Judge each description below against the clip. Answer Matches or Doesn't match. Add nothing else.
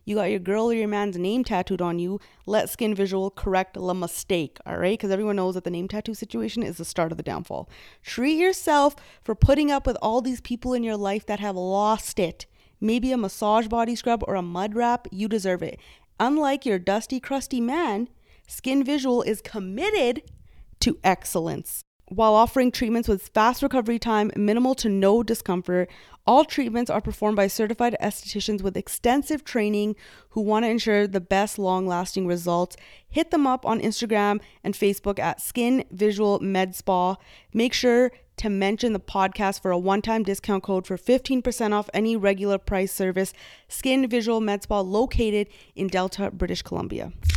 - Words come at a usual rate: Matches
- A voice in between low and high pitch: Doesn't match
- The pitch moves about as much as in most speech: Matches